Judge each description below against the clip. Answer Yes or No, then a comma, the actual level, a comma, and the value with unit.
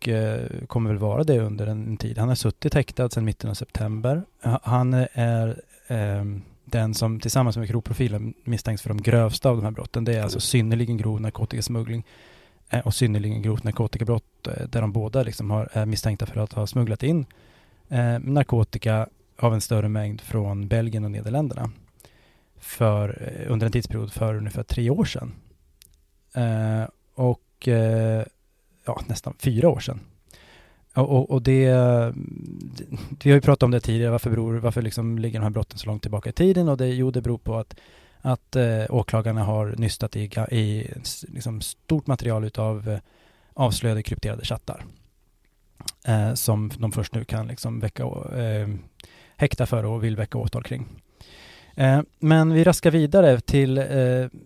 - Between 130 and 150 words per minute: No, average, 165 wpm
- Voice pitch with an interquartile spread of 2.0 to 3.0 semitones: Yes, narrow, 2.6 semitones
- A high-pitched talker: No, low, 115 Hz